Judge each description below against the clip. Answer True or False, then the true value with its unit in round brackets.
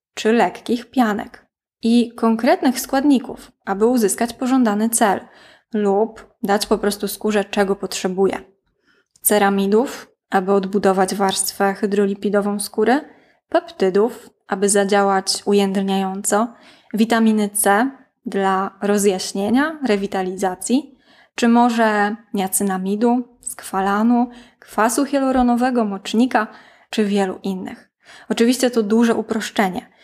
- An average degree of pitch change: True (3.2 semitones)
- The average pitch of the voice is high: True (215 Hz)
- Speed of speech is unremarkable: False (90 wpm)